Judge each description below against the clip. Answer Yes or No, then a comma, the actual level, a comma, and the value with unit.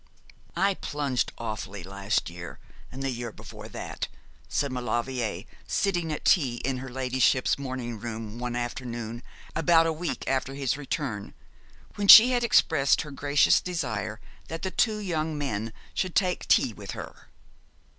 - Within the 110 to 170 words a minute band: Yes, average, 150 wpm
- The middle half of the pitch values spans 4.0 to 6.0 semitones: Yes, average, 5.2 semitones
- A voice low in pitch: Yes, low, 130 Hz